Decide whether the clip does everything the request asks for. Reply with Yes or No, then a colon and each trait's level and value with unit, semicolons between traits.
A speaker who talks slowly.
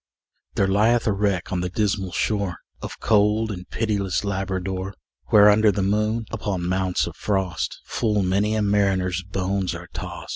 No: average, 160 wpm